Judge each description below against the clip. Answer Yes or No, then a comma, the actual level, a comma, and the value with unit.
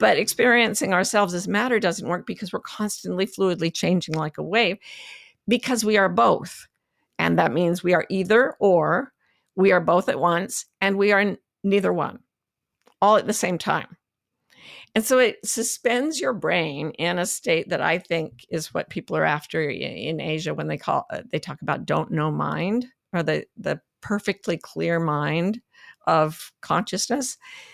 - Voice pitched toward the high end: Yes, high, 195 Hz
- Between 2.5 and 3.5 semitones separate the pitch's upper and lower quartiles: No, average, 4.8 semitones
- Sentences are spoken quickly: No, average, 170 wpm